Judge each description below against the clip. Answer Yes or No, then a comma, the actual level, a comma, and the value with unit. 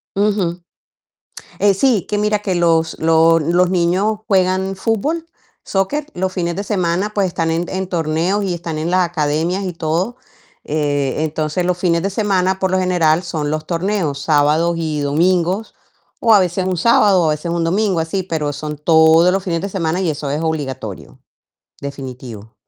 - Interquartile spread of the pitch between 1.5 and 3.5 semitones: Yes, average, 3.2 semitones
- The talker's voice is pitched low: No, medium, 175 Hz